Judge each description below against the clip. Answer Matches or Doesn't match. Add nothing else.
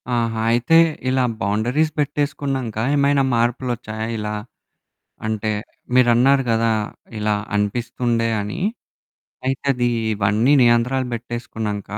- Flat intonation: Doesn't match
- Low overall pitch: Matches